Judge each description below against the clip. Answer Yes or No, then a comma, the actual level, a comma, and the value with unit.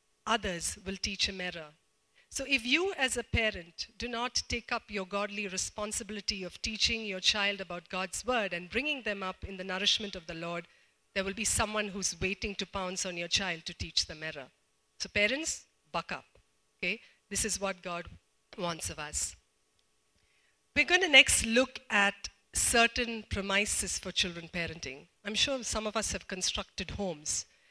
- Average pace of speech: Yes, average, 175 wpm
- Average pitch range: Yes, average, 3.4 semitones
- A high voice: Yes, high, 200 Hz